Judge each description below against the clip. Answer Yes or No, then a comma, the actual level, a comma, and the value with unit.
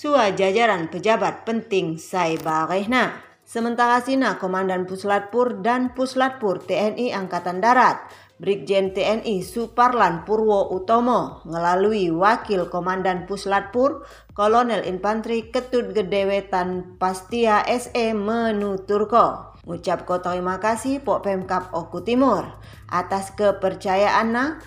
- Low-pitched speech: No, high, 205 Hz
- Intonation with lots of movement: No, average, 4.0 semitones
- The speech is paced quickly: No, average, 95 wpm